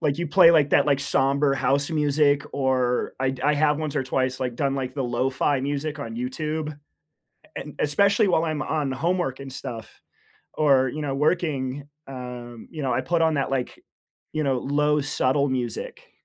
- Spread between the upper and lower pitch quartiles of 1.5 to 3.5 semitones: Yes, narrow, 2.4 semitones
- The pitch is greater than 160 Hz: No, medium, 140 Hz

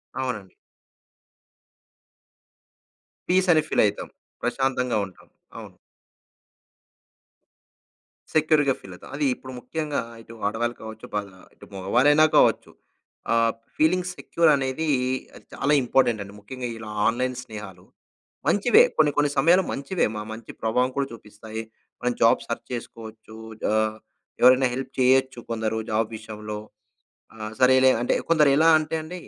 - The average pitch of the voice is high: No, low, 125 Hz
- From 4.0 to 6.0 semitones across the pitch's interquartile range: Yes, average, 4.8 semitones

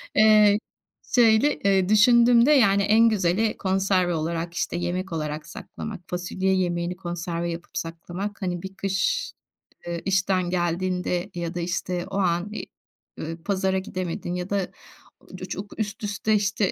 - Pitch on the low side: No, medium, 185 Hz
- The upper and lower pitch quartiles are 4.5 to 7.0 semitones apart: No, average, 2.8 semitones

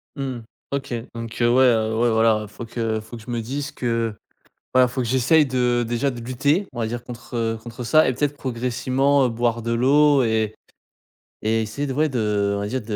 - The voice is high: No, low, 120 Hz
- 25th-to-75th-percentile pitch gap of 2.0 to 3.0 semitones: Yes, narrow, 2.6 semitones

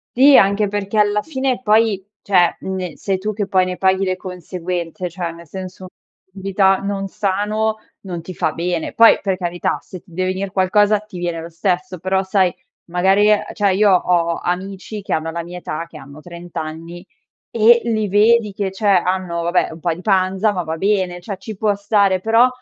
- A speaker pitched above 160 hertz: Yes, high, 190 Hz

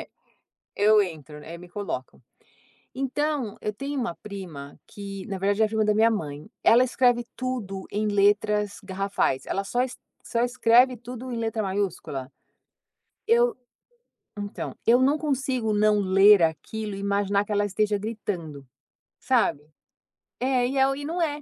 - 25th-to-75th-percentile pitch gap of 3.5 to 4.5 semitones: Yes, average, 4.0 semitones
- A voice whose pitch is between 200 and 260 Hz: Yes, high, 210 Hz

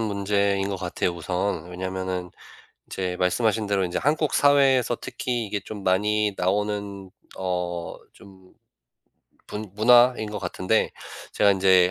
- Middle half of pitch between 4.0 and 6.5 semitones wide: No, narrow, 2.5 semitones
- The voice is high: No, low, 100 Hz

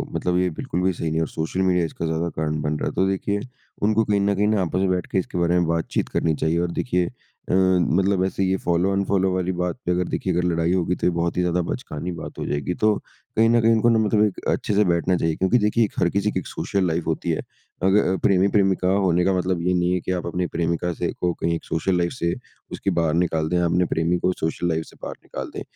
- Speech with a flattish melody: Yes, narrow, 2.2 semitones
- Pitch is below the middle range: Yes, very low, 90 Hz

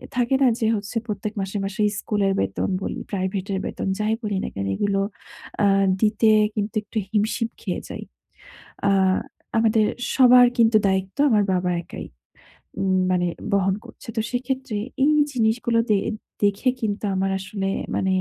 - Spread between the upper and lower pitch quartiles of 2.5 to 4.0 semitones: Yes, average, 2.8 semitones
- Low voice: No, high, 210 Hz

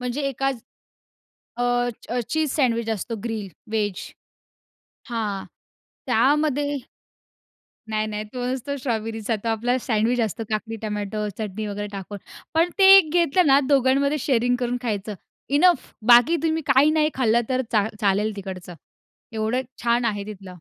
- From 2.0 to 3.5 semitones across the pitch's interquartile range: No, average, 4.2 semitones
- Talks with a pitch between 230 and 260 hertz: Yes, high, 235 Hz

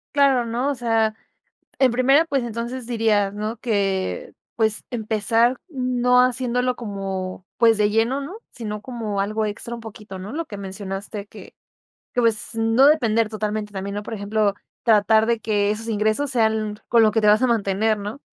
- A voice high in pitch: Yes, high, 220 Hz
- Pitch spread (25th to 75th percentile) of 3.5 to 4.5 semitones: No, average, 2.7 semitones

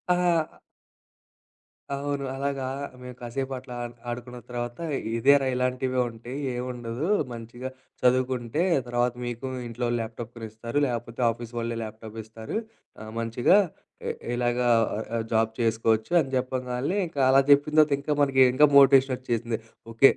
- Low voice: Yes, low, 125 Hz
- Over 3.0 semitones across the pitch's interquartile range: No, narrow, 2.5 semitones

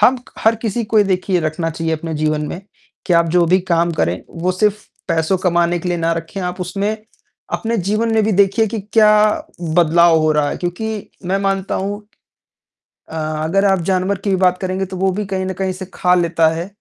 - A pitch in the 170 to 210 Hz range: Yes, medium, 185 Hz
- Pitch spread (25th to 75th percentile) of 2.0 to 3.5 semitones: Yes, average, 2.9 semitones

